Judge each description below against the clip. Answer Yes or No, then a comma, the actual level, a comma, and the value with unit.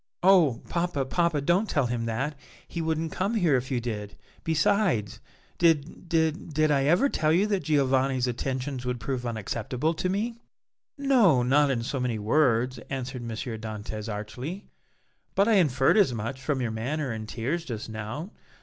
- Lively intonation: Yes, wide, 5.8 semitones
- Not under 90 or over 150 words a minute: No, average, 170 wpm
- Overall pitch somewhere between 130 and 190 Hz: Yes, low, 135 Hz